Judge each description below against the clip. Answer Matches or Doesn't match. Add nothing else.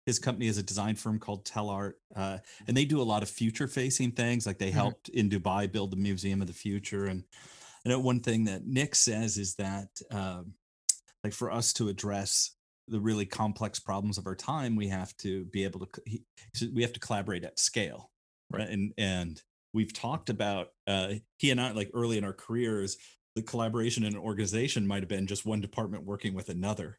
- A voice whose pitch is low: Matches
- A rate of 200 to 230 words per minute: Matches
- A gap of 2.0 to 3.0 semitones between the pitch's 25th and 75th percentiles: Matches